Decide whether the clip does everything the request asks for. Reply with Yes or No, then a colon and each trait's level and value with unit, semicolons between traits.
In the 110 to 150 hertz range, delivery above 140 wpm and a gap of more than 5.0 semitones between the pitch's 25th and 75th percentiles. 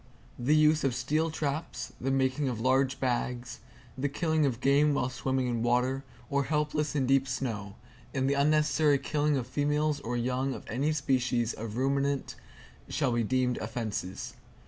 No: low, 135 Hz; average, 165 wpm; average, 2.8 semitones